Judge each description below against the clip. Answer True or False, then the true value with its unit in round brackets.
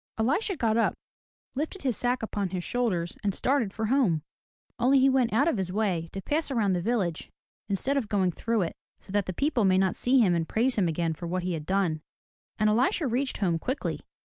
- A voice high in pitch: True (215 Hz)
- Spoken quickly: True (220 wpm)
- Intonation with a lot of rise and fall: True (5.7 semitones)